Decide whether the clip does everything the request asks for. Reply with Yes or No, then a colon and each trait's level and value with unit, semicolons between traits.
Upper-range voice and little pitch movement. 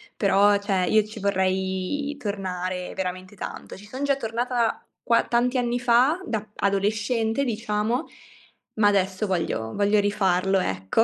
No: high, 205 Hz; average, 3.6 semitones